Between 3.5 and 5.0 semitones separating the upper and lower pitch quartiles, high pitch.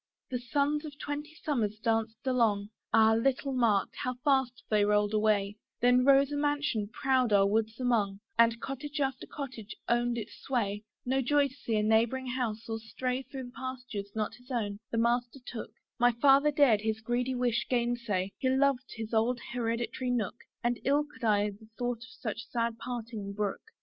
No: average, 3.1 semitones; high, 240 Hz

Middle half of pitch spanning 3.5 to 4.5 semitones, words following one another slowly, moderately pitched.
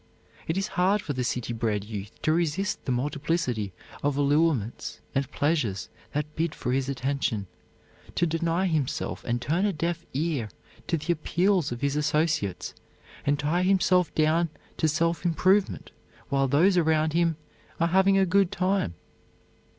No: average, 4.1 semitones; average, 155 wpm; medium, 155 Hz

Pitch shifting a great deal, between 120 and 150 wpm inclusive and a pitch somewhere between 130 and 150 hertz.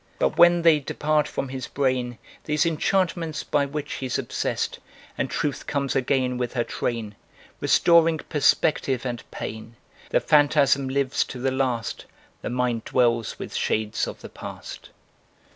No: average, 3.4 semitones; average, 145 wpm; low, 135 Hz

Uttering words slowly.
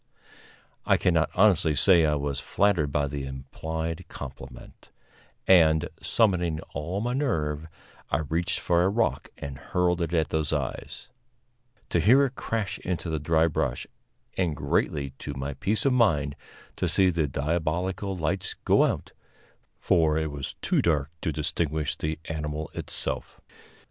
No: average, 150 wpm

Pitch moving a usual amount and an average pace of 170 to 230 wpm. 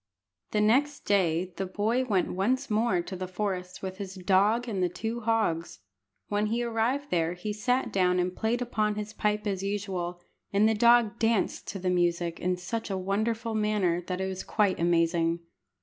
Yes: average, 3.6 semitones; average, 185 wpm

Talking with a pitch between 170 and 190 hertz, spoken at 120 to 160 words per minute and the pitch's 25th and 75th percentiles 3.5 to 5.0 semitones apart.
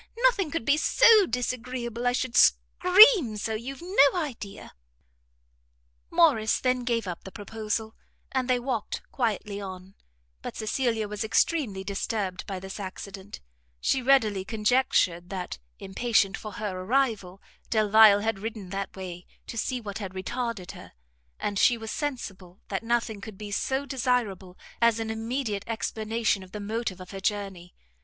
No: high, 220 Hz; average, 150 wpm; average, 4.1 semitones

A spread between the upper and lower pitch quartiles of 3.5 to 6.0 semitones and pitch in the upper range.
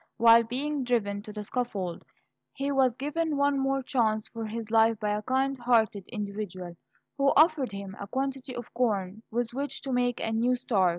Yes: average, 4.1 semitones; high, 235 Hz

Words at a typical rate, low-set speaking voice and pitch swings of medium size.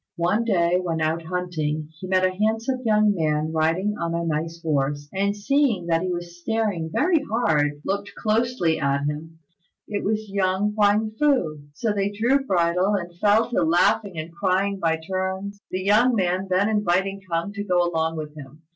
No: average, 180 wpm; medium, 185 Hz; average, 4.2 semitones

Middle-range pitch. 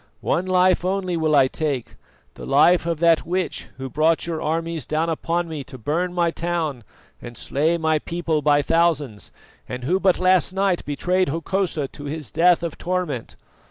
Yes: medium, 165 Hz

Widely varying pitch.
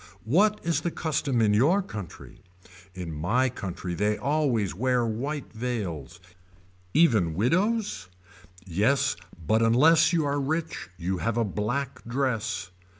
Yes: wide, 6.1 semitones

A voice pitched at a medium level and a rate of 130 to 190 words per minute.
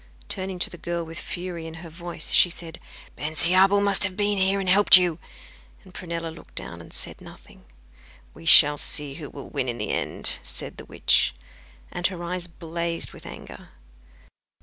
Yes: medium, 170 Hz; average, 180 wpm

